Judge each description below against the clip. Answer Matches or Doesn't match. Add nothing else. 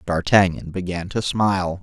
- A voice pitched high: Doesn't match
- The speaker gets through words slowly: Matches